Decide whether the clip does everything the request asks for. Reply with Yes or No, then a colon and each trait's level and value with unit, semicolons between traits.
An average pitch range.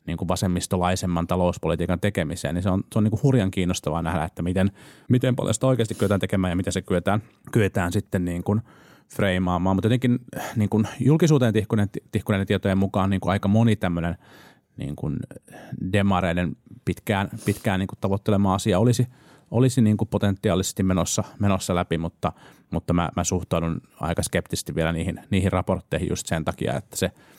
Yes: average, 3.5 semitones